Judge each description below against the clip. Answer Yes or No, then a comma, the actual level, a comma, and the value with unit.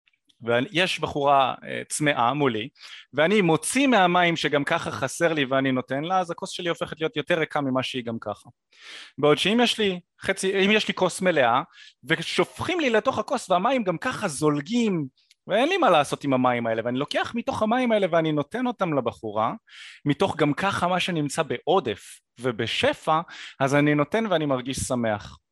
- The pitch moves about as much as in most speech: No, wide, 6.0 semitones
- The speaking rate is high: Yes, fast, 160 wpm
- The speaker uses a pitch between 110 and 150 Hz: No, medium, 160 Hz